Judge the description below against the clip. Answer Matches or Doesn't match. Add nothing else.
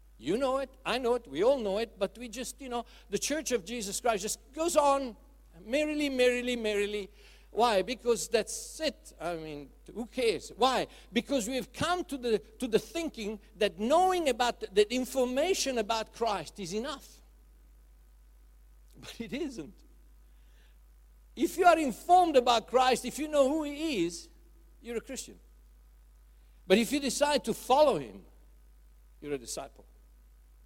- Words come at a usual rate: Matches